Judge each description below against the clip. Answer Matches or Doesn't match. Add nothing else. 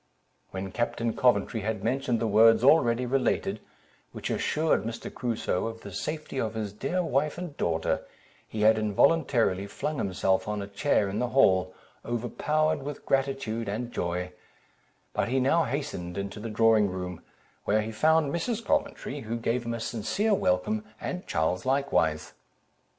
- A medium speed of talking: Matches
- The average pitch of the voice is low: Matches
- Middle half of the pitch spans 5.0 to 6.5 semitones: Matches